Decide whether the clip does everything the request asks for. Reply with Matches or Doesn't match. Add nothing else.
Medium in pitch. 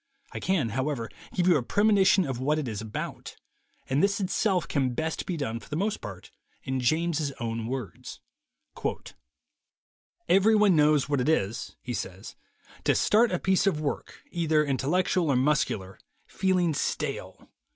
Matches